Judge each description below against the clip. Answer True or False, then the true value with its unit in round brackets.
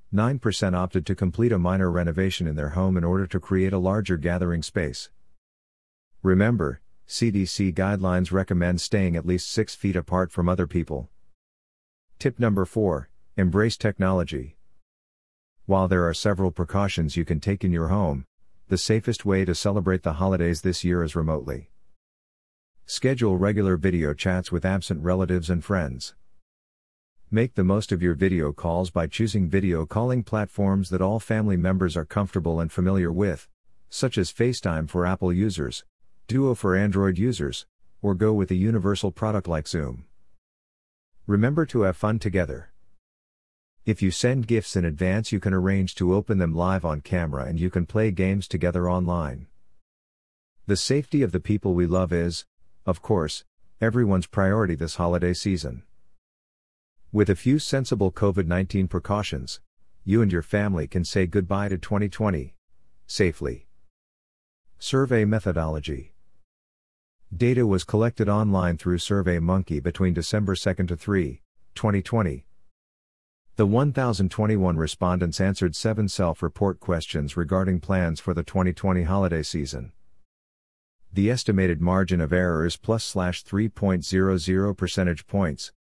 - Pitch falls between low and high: False (95 Hz)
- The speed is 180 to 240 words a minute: False (140 wpm)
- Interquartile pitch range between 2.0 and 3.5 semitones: True (3.0 semitones)